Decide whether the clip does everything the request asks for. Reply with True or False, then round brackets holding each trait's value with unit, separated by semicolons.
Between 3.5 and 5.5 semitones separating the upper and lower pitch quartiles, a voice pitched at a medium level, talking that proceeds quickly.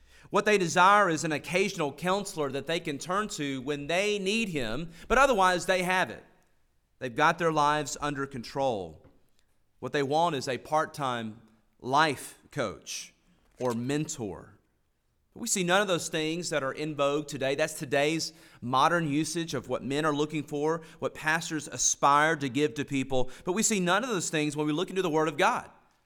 False (4.0 semitones; 155 Hz; 190 wpm)